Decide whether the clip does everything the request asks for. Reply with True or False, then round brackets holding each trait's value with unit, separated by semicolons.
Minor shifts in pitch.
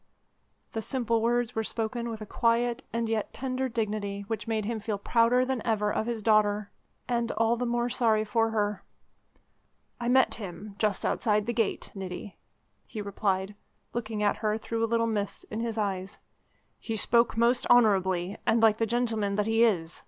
True (2.1 semitones)